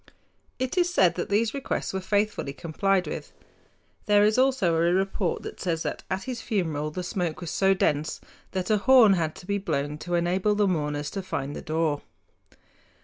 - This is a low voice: No, medium, 185 Hz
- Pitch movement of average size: Yes, average, 4.2 semitones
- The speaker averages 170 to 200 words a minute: Yes, average, 190 wpm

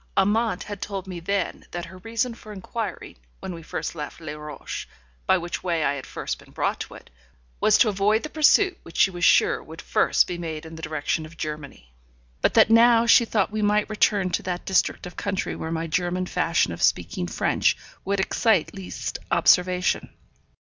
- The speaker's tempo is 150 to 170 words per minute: No, average, 195 wpm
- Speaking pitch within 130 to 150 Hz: No, medium, 185 Hz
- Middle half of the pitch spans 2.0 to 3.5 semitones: No, average, 4.3 semitones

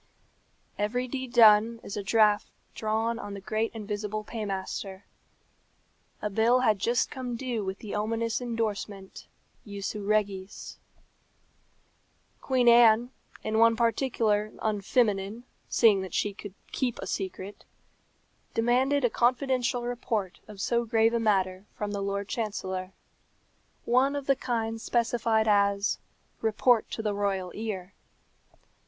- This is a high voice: Yes, high, 220 Hz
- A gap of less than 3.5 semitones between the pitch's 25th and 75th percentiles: Yes, average, 2.8 semitones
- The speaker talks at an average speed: No, slow, 125 wpm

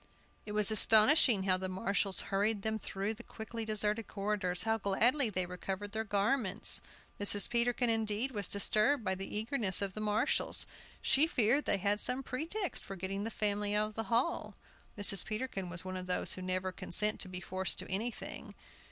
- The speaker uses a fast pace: No, average, 185 wpm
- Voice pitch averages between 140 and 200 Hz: No, high, 210 Hz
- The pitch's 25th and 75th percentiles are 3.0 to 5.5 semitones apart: No, narrow, 2.6 semitones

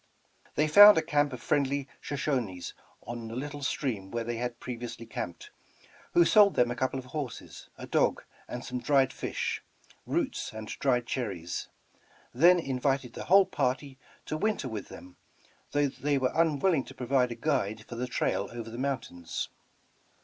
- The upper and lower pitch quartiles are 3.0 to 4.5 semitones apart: Yes, average, 3.7 semitones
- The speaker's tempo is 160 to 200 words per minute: Yes, average, 165 wpm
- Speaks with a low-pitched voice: Yes, low, 130 Hz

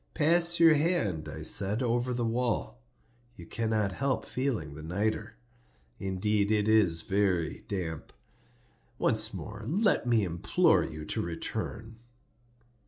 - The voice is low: Yes, low, 110 Hz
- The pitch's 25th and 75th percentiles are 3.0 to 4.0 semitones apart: No, average, 5.3 semitones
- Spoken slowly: Yes, slow, 125 wpm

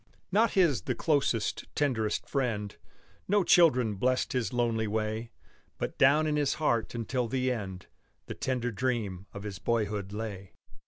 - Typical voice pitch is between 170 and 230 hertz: No, low, 120 Hz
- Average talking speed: Yes, average, 150 wpm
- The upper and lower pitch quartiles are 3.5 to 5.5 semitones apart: Yes, average, 4.1 semitones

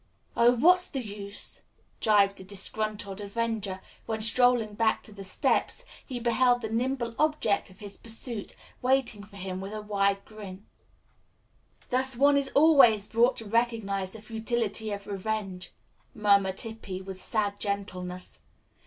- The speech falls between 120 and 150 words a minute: Yes, average, 145 wpm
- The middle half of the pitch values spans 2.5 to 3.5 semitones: Yes, average, 3.0 semitones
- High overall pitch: Yes, high, 215 Hz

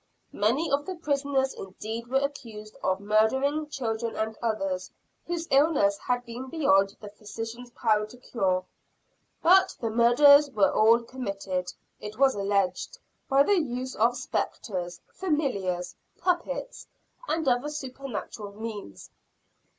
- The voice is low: No, high, 240 Hz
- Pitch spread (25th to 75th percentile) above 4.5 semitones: Yes, average, 5.0 semitones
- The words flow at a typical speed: No, slow, 125 wpm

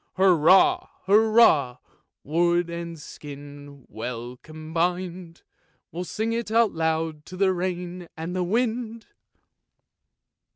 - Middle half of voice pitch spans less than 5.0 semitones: Yes, average, 3.3 semitones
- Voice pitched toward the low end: No, medium, 175 Hz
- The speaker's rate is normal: No, slow, 95 wpm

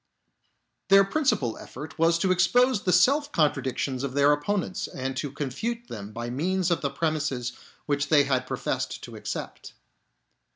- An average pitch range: No, wide, 5.9 semitones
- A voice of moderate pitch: Yes, medium, 150 Hz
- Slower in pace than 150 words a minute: No, average, 155 wpm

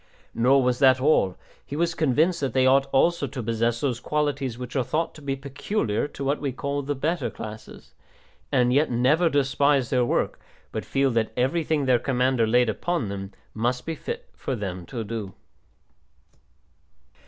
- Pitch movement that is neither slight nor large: Yes, average, 3.4 semitones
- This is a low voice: Yes, low, 130 Hz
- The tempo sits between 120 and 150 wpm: No, average, 175 wpm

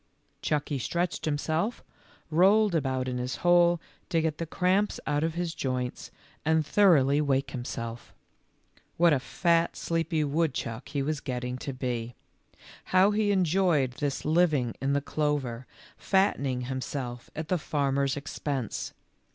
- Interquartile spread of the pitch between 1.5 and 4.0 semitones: No, average, 4.5 semitones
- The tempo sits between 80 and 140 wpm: Yes, slow, 135 wpm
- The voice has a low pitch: No, medium, 150 Hz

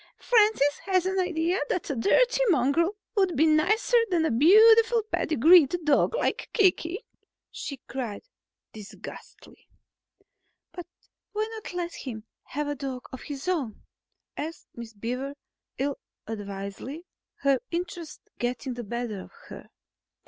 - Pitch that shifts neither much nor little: No, wide, 6.4 semitones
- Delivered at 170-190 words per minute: No, slow, 135 wpm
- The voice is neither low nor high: No, very high, 310 Hz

